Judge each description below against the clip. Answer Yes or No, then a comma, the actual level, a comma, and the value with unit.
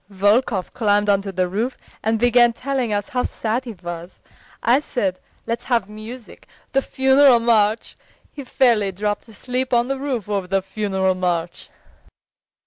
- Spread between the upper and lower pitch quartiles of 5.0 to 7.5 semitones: No, average, 4.1 semitones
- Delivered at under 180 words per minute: Yes, average, 150 wpm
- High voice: Yes, high, 220 Hz